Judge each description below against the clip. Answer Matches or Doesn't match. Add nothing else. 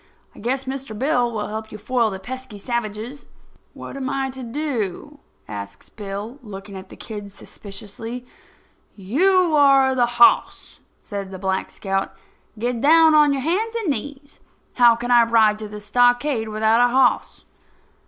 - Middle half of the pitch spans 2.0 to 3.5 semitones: Doesn't match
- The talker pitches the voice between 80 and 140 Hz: Doesn't match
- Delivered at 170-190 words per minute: Doesn't match